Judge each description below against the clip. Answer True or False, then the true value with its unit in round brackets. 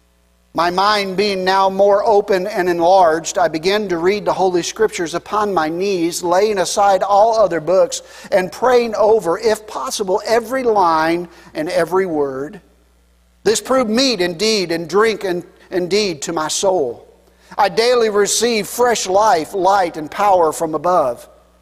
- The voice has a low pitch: False (190 Hz)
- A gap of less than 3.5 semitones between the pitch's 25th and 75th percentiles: False (4.1 semitones)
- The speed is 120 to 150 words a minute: True (145 wpm)